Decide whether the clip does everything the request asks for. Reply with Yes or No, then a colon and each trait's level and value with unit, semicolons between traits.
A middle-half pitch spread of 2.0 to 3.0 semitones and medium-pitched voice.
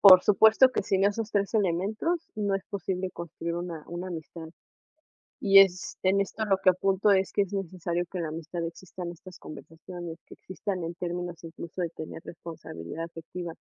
Yes: narrow, 2.6 semitones; medium, 180 Hz